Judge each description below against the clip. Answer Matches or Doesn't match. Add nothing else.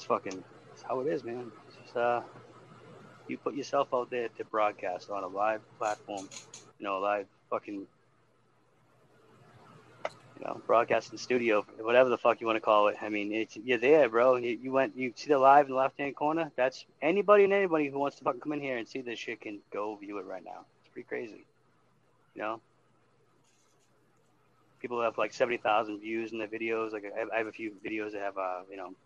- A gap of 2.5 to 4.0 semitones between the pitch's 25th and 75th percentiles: Matches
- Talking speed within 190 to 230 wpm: Matches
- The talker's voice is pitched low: Matches